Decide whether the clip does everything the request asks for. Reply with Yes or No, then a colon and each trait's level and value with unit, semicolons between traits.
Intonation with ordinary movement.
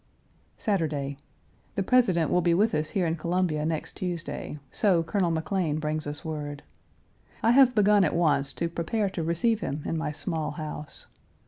Yes: average, 4.0 semitones